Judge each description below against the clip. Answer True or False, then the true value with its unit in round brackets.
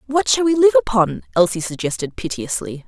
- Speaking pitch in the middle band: False (225 Hz)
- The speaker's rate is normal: True (165 wpm)